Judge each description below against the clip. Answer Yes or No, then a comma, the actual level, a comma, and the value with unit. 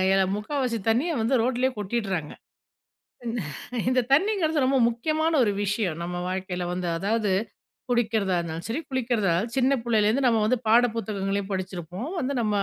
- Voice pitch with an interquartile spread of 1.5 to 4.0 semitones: No, average, 5.0 semitones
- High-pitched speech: Yes, high, 225 Hz